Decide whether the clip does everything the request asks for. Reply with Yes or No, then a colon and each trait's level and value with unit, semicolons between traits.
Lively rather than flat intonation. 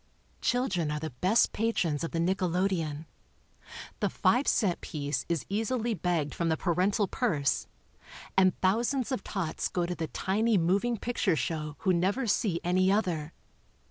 No: average, 4.5 semitones